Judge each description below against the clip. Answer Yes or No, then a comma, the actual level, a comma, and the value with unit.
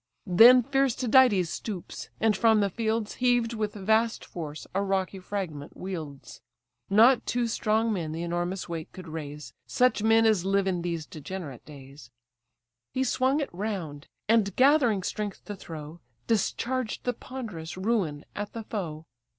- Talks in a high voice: Yes, high, 200 Hz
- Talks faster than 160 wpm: No, average, 150 wpm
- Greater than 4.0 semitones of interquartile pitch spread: Yes, average, 5.1 semitones